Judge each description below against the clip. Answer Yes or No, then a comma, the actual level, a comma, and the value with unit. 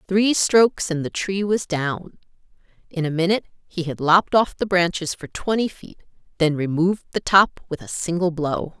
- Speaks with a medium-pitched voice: Yes, medium, 175 Hz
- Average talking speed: Yes, average, 185 wpm